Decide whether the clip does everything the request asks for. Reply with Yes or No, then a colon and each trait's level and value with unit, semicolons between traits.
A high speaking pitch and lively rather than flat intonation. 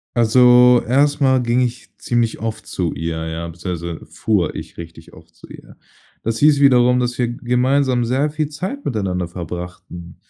No: low, 120 Hz; wide, 6.5 semitones